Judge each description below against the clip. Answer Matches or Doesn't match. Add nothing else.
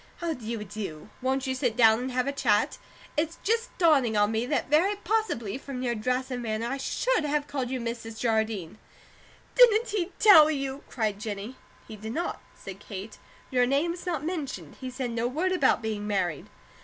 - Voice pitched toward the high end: Matches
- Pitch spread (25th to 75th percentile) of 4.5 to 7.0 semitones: Matches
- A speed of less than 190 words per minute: Doesn't match